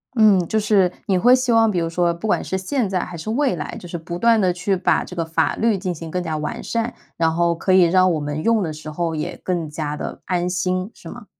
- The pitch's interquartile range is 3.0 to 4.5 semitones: Yes, average, 4.1 semitones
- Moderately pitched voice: Yes, medium, 180 Hz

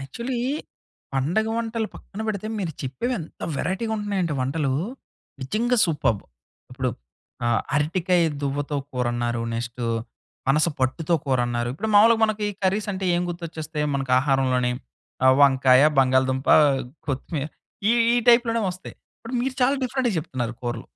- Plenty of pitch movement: Yes, wide, 8.3 semitones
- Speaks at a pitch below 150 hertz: No, medium, 155 Hz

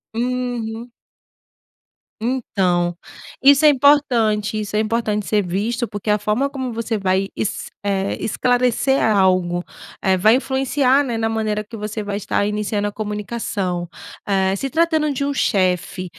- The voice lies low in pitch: No, high, 215 Hz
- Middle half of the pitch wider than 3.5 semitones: Yes, average, 3.9 semitones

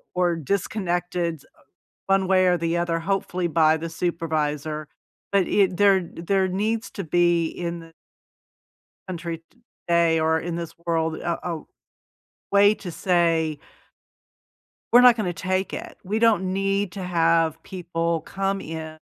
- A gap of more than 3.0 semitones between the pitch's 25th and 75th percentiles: No, average, 2.7 semitones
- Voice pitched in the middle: Yes, medium, 175 Hz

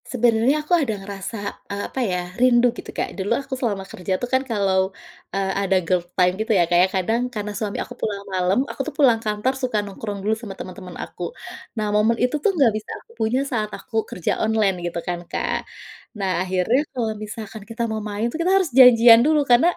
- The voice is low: No, high, 215 Hz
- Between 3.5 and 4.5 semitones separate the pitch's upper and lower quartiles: Yes, average, 3.9 semitones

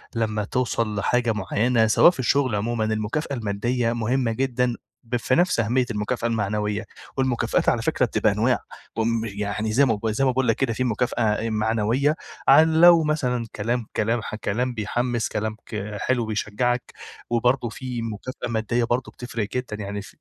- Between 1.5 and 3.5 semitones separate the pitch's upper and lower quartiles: Yes, average, 2.7 semitones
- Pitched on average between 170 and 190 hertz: No, low, 115 Hz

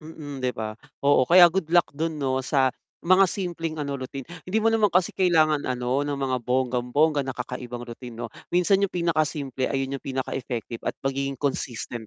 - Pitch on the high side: No, medium, 140 Hz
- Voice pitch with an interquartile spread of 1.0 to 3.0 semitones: No, average, 4.6 semitones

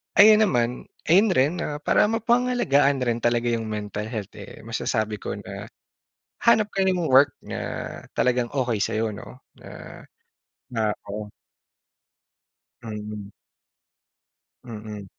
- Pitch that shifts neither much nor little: No, wide, 7.5 semitones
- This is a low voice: Yes, low, 120 Hz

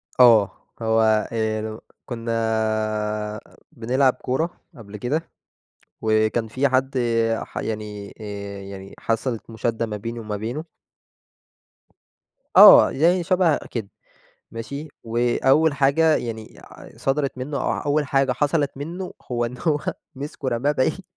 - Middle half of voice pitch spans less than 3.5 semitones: No, average, 4.4 semitones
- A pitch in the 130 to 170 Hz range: No, low, 120 Hz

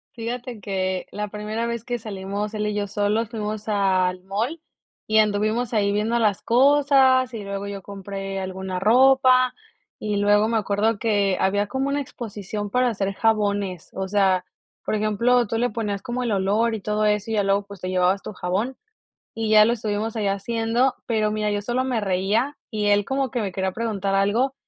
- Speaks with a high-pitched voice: Yes, high, 210 Hz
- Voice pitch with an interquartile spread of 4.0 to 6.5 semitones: No, average, 2.7 semitones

